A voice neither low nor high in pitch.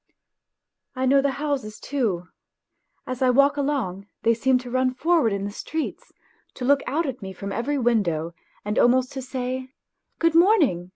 No: very high, 255 Hz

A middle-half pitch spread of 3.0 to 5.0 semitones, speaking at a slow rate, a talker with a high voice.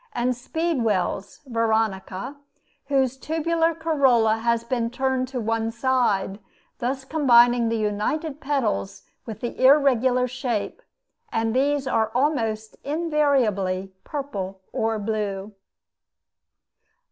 Yes: average, 3.9 semitones; slow, 100 wpm; high, 240 Hz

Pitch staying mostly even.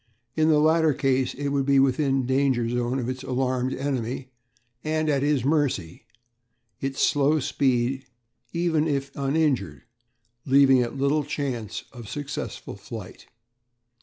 Yes: narrow, 2.3 semitones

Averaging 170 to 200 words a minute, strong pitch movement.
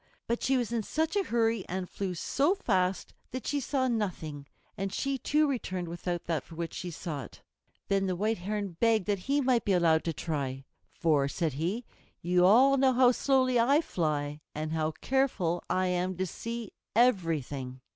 Yes: average, 185 wpm; wide, 6.7 semitones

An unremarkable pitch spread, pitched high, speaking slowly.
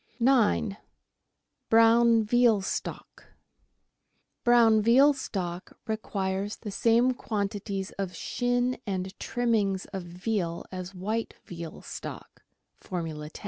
Yes: average, 3.8 semitones; high, 210 Hz; slow, 100 wpm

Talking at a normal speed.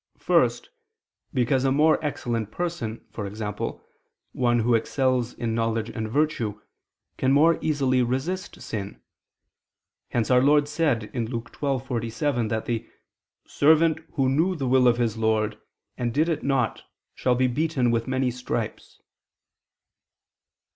No: slow, 130 wpm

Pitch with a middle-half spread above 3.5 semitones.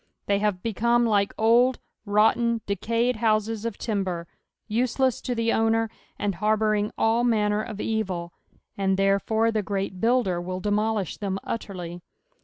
No: narrow, 2.4 semitones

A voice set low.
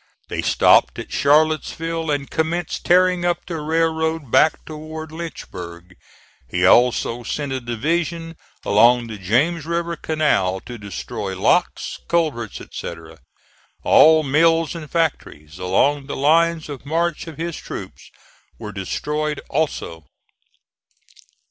No: medium, 150 Hz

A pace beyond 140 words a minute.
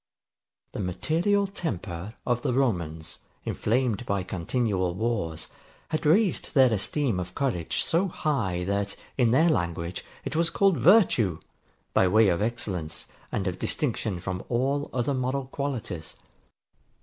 No: slow, 135 wpm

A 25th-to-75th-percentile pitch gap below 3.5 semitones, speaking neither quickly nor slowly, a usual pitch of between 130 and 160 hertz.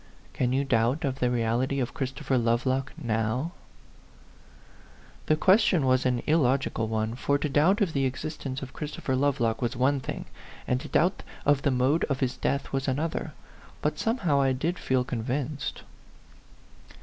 Yes: average, 2.8 semitones; average, 165 wpm; low, 135 Hz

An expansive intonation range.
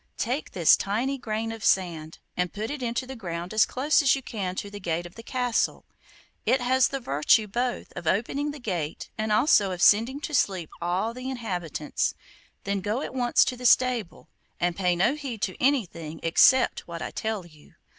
Yes: wide, 6.0 semitones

